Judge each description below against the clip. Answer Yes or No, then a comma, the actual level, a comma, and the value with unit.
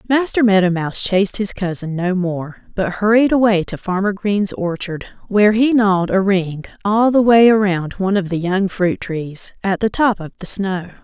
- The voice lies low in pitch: No, high, 195 Hz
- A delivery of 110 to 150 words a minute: No, average, 195 wpm